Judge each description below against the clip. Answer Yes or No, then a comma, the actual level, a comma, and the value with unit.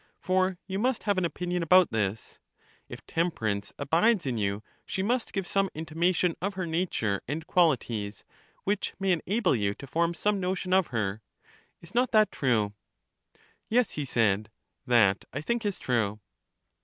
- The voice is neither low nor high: Yes, medium, 170 Hz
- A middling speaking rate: Yes, average, 165 wpm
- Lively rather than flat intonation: Yes, wide, 8.8 semitones